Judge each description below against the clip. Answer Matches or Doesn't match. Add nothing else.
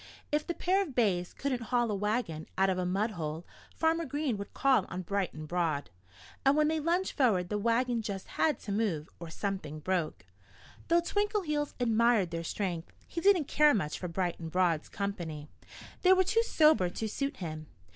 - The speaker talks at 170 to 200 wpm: Matches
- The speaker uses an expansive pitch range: Matches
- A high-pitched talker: Matches